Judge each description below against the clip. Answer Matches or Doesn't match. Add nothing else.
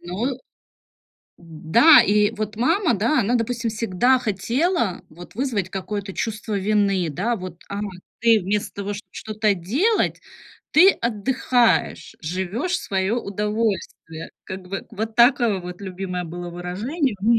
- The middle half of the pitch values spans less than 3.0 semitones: Doesn't match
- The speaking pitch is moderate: Doesn't match